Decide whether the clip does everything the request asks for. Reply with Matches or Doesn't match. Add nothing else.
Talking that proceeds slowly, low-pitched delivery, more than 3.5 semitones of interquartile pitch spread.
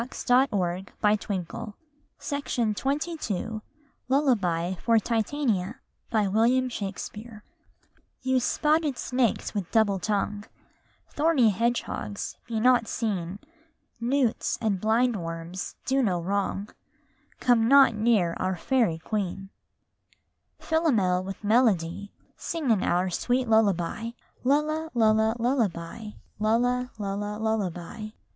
Doesn't match